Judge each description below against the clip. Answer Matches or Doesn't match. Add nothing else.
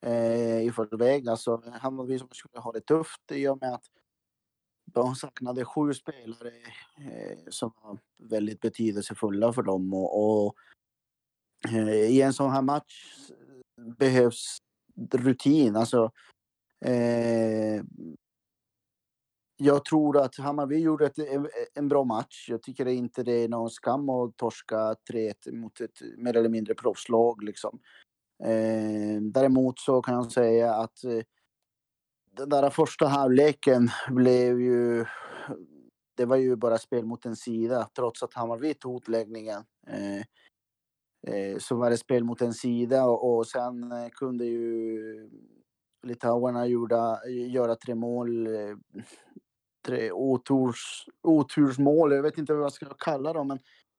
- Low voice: Matches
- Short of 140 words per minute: Matches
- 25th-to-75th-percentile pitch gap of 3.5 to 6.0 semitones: Doesn't match